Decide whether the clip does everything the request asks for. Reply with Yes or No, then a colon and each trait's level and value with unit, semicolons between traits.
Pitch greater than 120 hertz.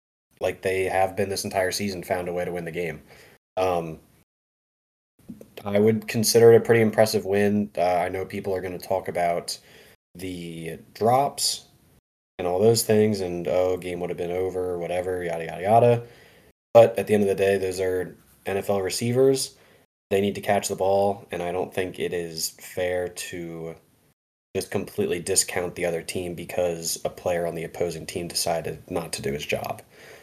No: very low, 95 Hz